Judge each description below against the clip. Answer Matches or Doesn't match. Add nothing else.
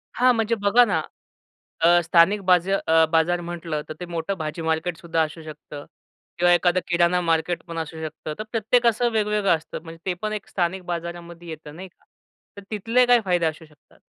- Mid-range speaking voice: Matches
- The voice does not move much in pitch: Doesn't match